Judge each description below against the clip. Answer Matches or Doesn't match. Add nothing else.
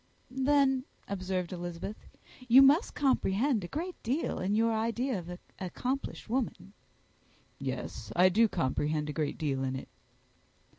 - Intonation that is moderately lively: Doesn't match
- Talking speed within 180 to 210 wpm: Doesn't match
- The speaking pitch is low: Doesn't match